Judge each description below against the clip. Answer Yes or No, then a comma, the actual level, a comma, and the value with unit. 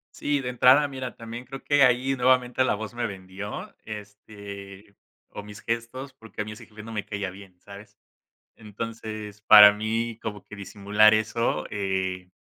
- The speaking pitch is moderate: No, low, 110 Hz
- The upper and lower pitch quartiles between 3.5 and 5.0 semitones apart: No, narrow, 2.6 semitones